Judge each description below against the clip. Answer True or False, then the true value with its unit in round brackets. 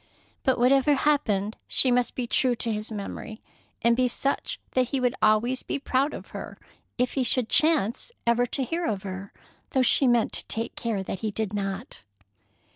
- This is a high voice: True (240 Hz)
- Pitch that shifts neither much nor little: True (3.4 semitones)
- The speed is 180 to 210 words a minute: True (190 wpm)